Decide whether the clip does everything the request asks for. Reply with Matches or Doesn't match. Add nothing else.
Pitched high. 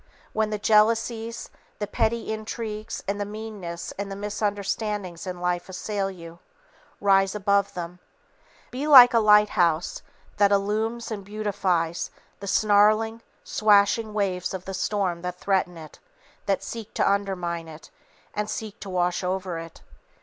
Matches